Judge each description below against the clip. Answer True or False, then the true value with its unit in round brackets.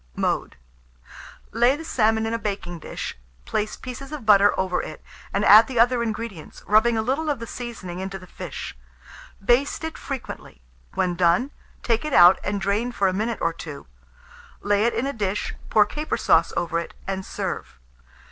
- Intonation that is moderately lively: True (4.1 semitones)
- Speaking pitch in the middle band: False (215 Hz)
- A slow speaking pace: False (180 wpm)